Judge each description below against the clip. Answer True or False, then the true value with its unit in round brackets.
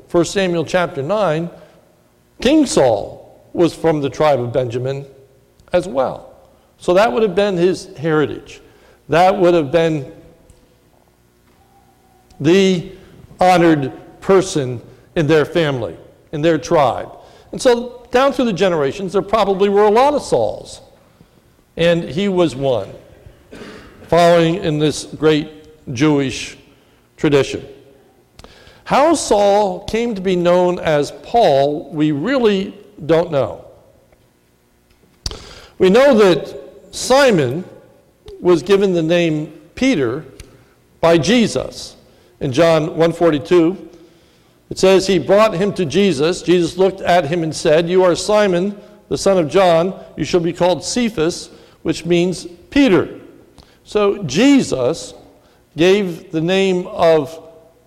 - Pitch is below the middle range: False (170 Hz)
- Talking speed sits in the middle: False (120 wpm)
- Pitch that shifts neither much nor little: True (3.9 semitones)